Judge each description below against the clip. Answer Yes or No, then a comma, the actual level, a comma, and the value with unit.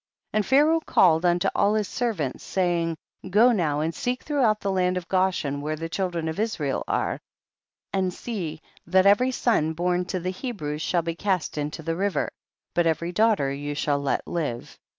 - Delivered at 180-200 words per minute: Yes, average, 185 wpm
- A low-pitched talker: No, medium, 180 Hz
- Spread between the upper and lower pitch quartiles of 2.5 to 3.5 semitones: No, average, 4.2 semitones